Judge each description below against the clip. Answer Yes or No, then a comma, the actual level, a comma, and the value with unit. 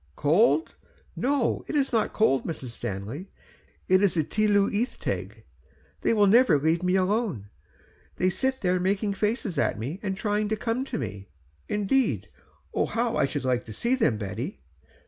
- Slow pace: No, average, 165 wpm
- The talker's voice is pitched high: Yes, high, 195 Hz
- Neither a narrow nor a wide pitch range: No, wide, 7.8 semitones